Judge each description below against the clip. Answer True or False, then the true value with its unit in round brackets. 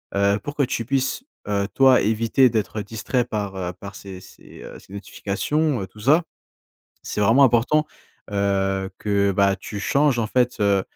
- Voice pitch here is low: True (105 Hz)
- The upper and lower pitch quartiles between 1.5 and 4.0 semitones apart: False (4.4 semitones)